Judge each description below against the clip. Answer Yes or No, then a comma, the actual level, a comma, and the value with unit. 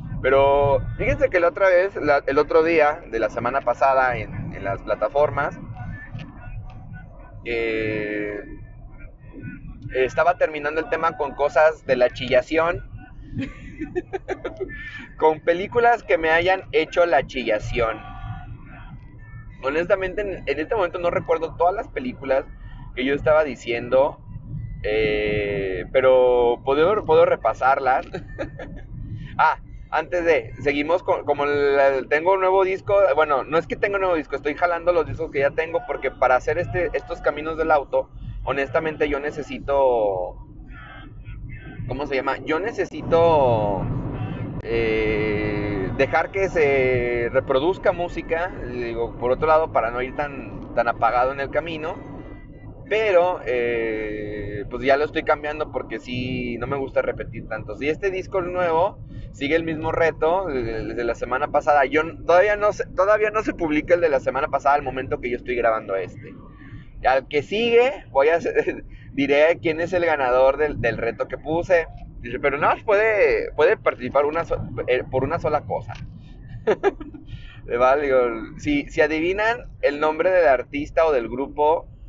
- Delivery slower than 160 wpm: Yes, average, 150 wpm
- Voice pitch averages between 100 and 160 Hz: Yes, medium, 140 Hz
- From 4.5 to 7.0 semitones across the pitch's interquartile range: Yes, average, 5.3 semitones